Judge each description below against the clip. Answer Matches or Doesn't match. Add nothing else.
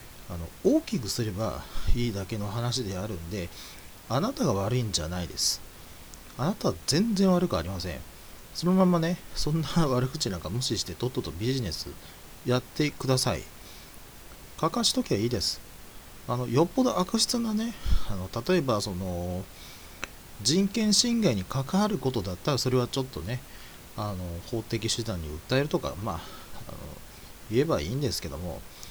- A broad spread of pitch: Matches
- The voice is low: Matches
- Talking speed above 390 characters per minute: Doesn't match